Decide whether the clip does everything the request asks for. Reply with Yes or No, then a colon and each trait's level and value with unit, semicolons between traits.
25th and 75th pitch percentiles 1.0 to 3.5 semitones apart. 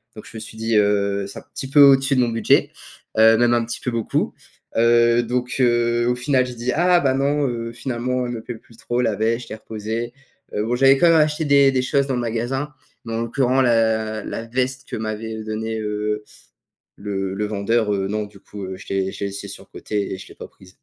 Yes: average, 2.9 semitones